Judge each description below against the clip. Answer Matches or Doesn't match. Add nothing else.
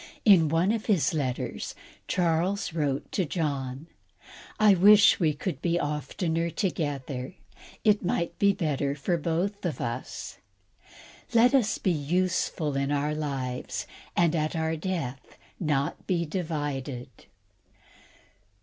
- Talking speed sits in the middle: Doesn't match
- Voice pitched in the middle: Matches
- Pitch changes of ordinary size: Matches